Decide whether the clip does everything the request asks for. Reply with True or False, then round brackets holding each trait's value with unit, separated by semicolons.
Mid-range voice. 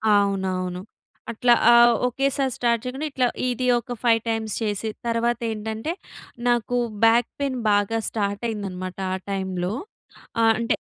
False (225 Hz)